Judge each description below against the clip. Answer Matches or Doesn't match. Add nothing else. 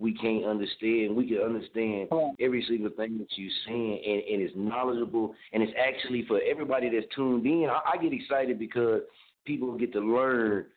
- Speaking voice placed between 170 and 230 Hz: Doesn't match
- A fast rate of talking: Doesn't match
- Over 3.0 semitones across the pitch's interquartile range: Doesn't match